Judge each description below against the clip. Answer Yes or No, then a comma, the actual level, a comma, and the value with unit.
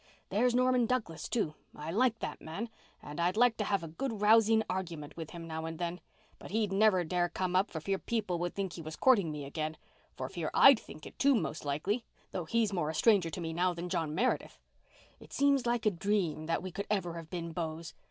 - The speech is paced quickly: Yes, fast, 220 wpm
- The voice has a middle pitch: Yes, medium, 180 Hz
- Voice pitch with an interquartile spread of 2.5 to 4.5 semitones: No, average, 5.0 semitones